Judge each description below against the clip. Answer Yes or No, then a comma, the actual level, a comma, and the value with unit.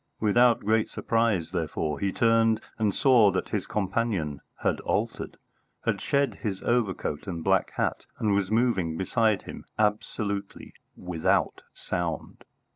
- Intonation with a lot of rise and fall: No, average, 3.5 semitones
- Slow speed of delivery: Yes, slow, 130 wpm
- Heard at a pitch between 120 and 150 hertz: No, low, 105 Hz